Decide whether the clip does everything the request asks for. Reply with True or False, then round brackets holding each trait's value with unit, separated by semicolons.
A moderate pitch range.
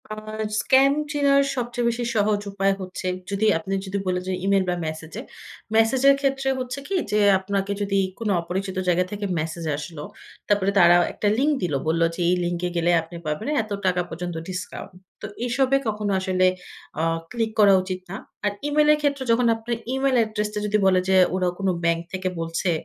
True (4.6 semitones)